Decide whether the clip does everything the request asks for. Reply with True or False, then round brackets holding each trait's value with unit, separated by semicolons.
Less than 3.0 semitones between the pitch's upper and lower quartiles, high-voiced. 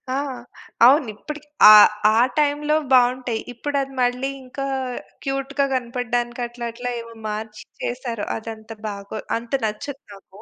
False (3.3 semitones; 245 Hz)